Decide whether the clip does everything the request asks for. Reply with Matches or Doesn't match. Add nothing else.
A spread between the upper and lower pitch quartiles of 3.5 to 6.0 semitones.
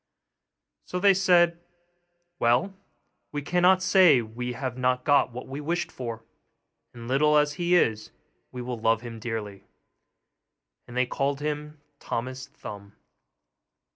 Matches